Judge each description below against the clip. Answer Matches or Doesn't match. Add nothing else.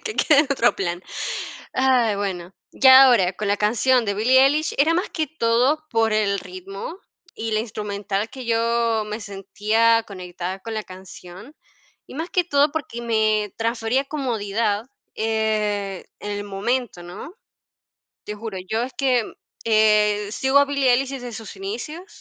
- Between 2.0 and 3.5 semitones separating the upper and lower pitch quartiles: Doesn't match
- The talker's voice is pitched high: Matches